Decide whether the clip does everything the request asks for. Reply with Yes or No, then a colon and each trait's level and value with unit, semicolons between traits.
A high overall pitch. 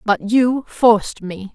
Yes: high, 220 Hz